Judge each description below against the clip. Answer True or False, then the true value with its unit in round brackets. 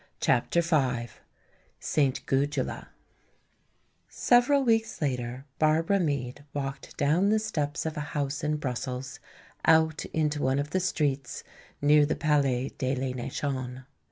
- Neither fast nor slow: False (130 wpm)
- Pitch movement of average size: True (3.2 semitones)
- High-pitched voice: False (145 Hz)